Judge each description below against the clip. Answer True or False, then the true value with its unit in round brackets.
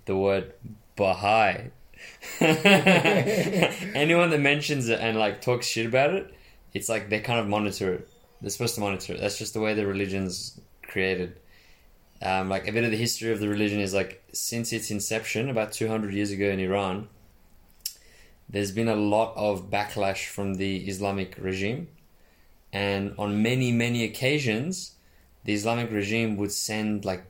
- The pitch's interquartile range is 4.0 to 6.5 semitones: False (3.0 semitones)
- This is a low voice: True (105 Hz)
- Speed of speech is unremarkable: True (165 wpm)